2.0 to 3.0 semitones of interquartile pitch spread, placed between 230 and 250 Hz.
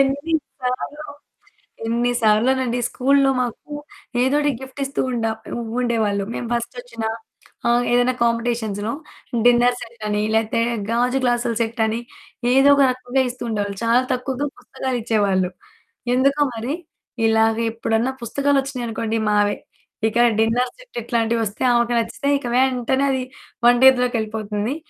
Yes: narrow, 2.6 semitones; high, 240 Hz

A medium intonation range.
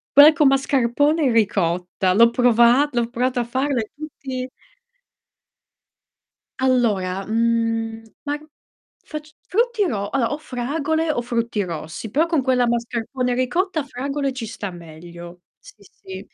Yes: average, 4.3 semitones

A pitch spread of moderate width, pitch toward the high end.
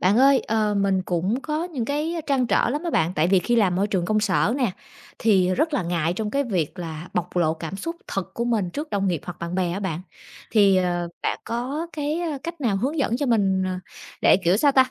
No: wide, 6.6 semitones; high, 205 Hz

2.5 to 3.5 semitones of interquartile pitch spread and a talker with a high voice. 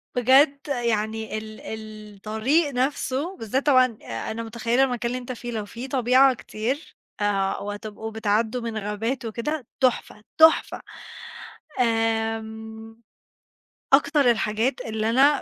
Yes: average, 3.0 semitones; high, 230 Hz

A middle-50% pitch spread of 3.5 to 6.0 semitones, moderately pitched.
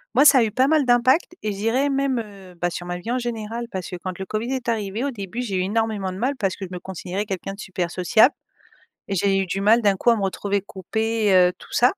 No: average, 3.9 semitones; high, 210 Hz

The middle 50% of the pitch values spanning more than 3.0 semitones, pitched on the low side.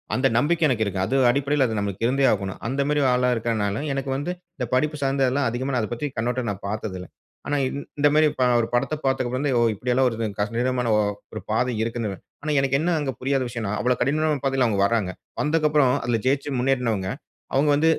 Yes: average, 3.6 semitones; low, 125 Hz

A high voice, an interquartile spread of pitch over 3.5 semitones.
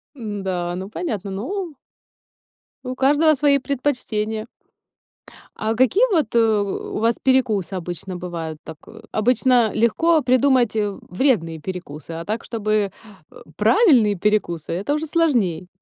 Yes: high, 220 Hz; wide, 5.6 semitones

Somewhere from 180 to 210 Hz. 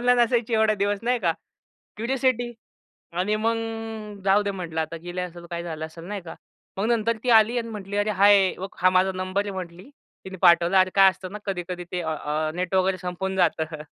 Yes: high, 190 Hz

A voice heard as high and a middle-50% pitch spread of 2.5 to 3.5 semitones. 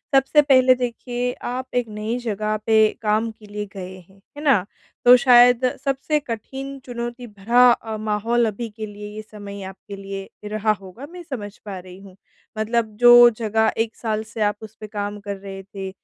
Yes: high, 220 Hz; average, 2.9 semitones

